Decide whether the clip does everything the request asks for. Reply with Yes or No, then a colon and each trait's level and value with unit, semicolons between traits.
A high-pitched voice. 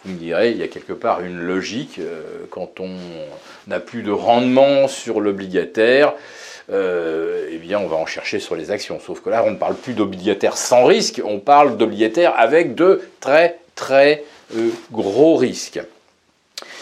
No: medium, 140 Hz